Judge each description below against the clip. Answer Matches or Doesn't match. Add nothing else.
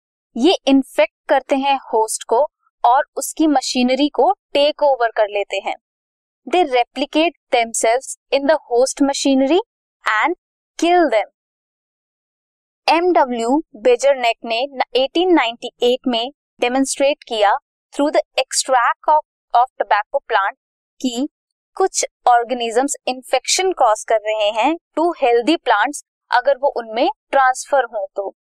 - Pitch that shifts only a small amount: Doesn't match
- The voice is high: Matches